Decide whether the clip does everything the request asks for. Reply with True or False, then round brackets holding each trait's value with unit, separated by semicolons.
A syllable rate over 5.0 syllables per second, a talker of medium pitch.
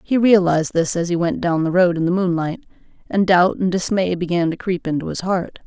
True (5.6 syllables/s; 175 Hz)